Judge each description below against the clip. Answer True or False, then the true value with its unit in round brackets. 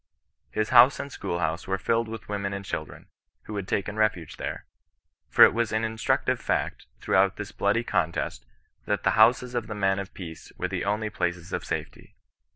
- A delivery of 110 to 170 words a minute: False (185 wpm)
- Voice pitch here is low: True (105 Hz)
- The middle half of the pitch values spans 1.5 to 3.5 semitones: True (2.6 semitones)